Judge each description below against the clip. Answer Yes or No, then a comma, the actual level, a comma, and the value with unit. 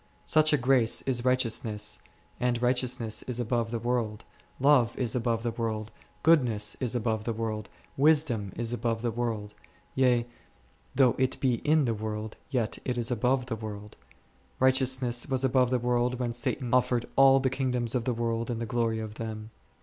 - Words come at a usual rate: Yes, average, 180 wpm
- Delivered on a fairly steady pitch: Yes, narrow, 2.2 semitones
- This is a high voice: No, low, 120 Hz